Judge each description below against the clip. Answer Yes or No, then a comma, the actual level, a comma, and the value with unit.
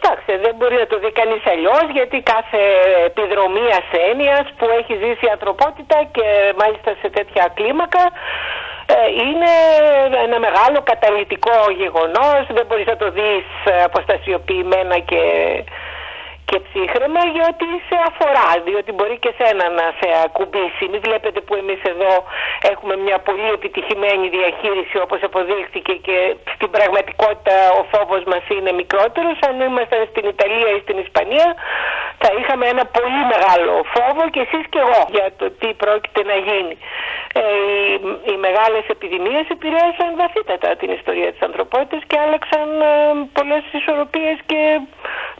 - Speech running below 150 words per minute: Yes, average, 140 wpm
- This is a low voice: No, high, 225 Hz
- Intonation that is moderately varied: No, wide, 7.1 semitones